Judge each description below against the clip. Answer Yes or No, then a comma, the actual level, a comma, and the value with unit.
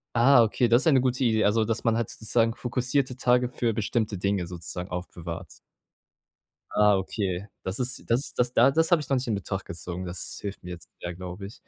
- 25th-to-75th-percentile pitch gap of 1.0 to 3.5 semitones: No, average, 5.0 semitones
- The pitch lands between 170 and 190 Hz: No, low, 110 Hz